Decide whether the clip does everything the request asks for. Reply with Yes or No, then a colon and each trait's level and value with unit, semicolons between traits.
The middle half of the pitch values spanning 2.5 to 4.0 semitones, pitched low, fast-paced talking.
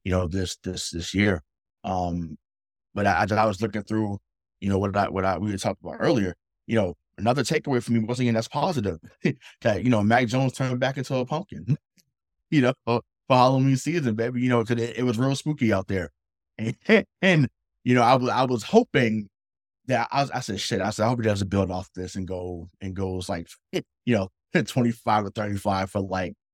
No: average, 4.8 semitones; low, 110 Hz; fast, 225 wpm